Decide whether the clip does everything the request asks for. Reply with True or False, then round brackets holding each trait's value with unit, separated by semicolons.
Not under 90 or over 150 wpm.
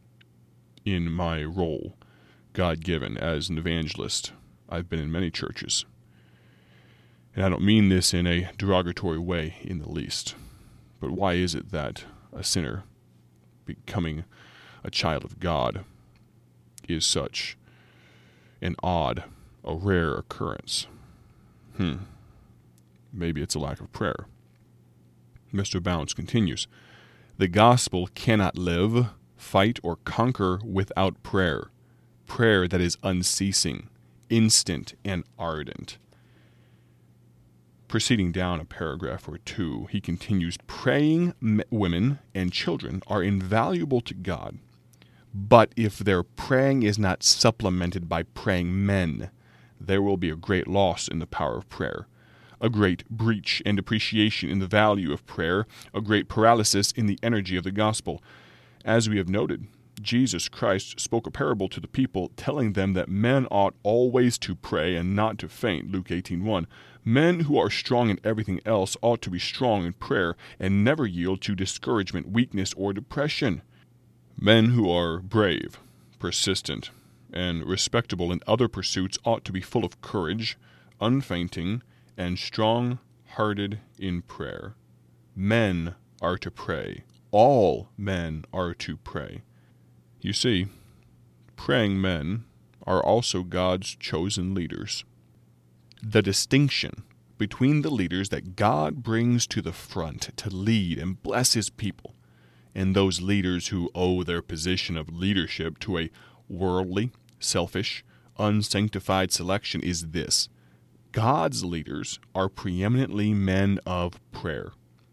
True (135 wpm)